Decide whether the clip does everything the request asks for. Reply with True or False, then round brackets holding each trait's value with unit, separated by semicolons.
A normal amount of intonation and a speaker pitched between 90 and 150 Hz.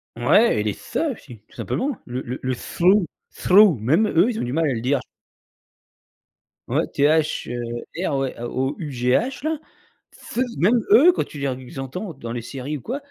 False (8.2 semitones; 140 Hz)